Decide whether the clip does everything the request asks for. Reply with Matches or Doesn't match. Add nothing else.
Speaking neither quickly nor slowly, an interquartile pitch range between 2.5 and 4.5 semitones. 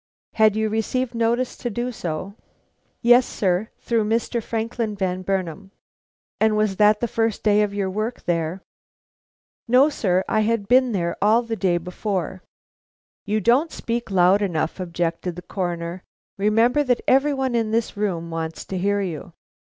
Matches